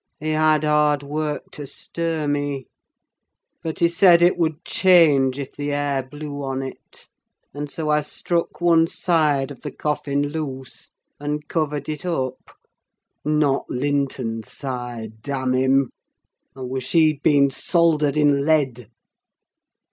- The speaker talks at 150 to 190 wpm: No, slow, 135 wpm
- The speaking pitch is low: No, medium, 145 Hz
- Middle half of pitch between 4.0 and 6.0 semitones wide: No, narrow, 2.5 semitones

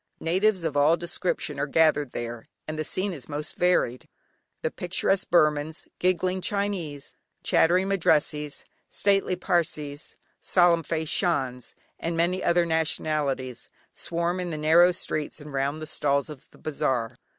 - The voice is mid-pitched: Yes, medium, 160 Hz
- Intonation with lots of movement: No, average, 3.3 semitones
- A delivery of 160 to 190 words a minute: No, average, 140 wpm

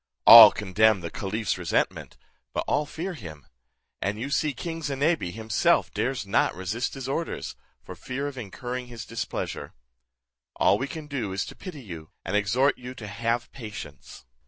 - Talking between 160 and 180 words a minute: Yes, average, 165 wpm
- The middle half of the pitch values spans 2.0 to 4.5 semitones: No, average, 5.3 semitones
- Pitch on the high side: No, low, 120 Hz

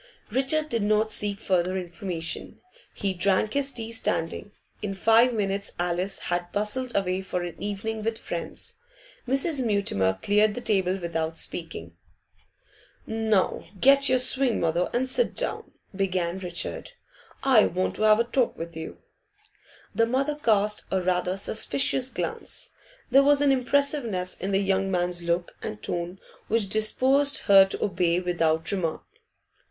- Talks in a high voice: Yes, high, 200 Hz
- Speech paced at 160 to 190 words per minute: No, average, 145 wpm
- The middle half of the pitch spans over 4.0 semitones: Yes, average, 4.7 semitones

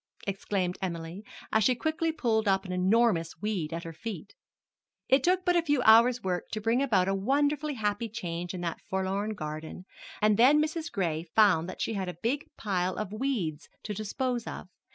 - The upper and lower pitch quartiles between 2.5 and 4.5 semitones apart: No, average, 5.3 semitones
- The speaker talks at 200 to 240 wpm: No, average, 190 wpm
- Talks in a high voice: Yes, high, 210 Hz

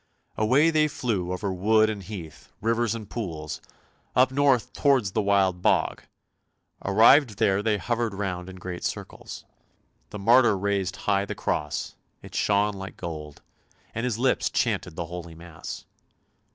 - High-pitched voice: No, low, 100 Hz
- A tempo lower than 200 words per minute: Yes, average, 150 wpm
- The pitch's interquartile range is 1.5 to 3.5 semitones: No, average, 4.0 semitones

